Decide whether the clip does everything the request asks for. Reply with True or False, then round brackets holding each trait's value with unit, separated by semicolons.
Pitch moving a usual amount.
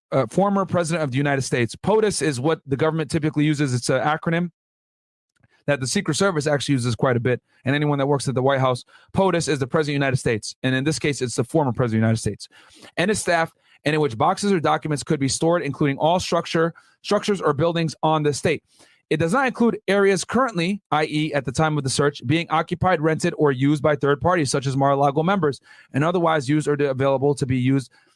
True (3.3 semitones)